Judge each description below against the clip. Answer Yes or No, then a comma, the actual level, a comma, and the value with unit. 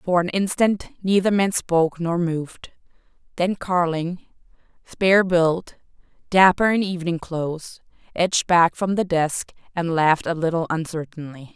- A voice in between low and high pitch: Yes, medium, 175 Hz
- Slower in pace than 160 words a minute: Yes, slow, 135 wpm